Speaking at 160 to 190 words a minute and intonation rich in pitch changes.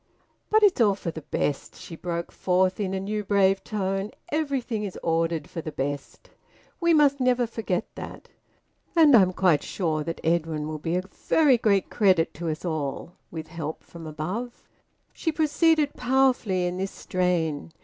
Yes: average, 170 wpm; wide, 6.5 semitones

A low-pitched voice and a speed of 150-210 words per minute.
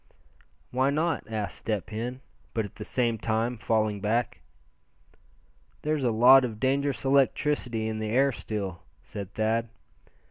No: low, 115 Hz; average, 140 wpm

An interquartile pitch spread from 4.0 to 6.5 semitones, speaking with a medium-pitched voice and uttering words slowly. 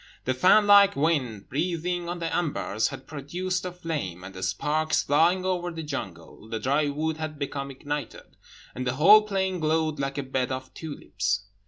No: average, 5.1 semitones; medium, 150 Hz; average, 180 wpm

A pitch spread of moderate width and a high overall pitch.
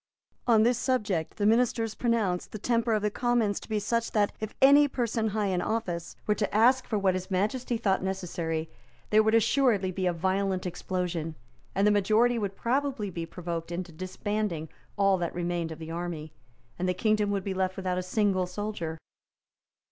Yes: average, 3.7 semitones; high, 200 Hz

